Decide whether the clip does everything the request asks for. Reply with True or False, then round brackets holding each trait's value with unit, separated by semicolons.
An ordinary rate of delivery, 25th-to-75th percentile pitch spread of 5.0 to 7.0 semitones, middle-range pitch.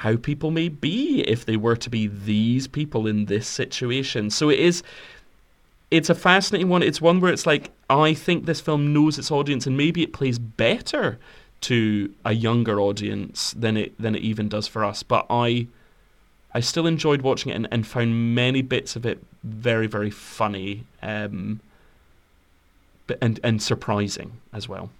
False (180 wpm; 5.4 semitones; 115 Hz)